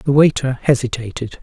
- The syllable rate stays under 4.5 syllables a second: No, 5.0 syllables/s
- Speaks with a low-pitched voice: Yes, low, 130 Hz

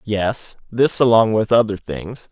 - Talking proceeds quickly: No, average, 155 wpm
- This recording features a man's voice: Yes, male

